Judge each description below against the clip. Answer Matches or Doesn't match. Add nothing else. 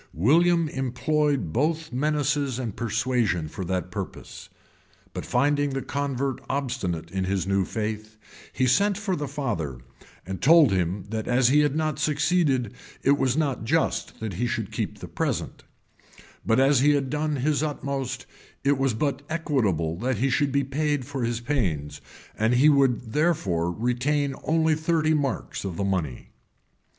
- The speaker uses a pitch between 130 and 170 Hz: Matches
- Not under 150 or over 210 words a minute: Matches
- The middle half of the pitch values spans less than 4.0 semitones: Doesn't match